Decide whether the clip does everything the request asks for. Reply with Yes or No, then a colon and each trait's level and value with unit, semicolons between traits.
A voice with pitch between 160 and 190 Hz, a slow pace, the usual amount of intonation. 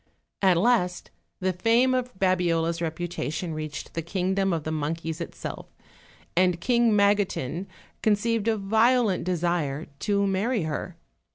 Yes: medium, 185 Hz; slow, 130 wpm; average, 3.9 semitones